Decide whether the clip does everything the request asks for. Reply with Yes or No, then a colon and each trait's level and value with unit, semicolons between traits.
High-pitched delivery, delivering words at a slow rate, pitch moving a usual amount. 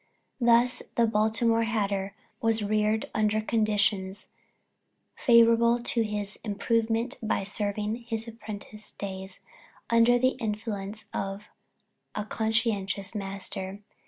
No: high, 215 Hz; slow, 100 wpm; narrow, 2.1 semitones